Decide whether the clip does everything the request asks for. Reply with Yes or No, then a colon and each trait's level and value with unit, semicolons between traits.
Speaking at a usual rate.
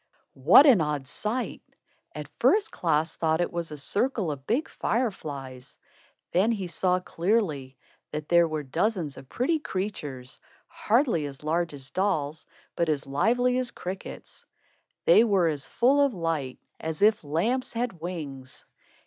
Yes: average, 150 wpm